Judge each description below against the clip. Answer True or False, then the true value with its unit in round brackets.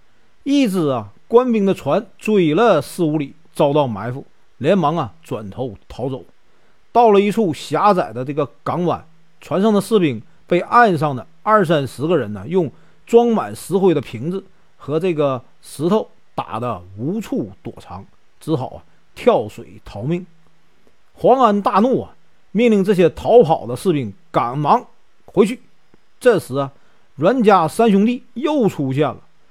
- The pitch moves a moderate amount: False (7.5 semitones)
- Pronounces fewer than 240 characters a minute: True (215 characters per minute)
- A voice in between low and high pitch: True (165 Hz)